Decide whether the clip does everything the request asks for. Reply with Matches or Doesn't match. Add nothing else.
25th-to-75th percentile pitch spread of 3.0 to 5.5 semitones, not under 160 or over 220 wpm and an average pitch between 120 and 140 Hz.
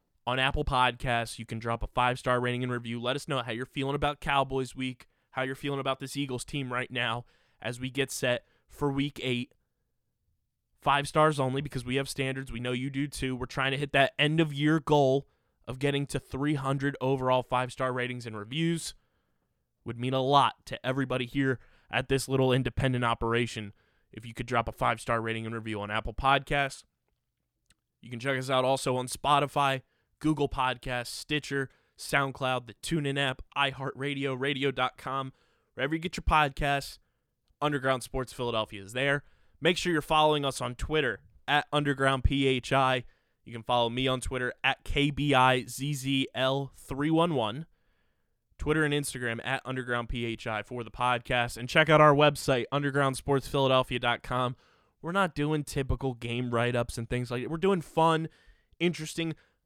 Doesn't match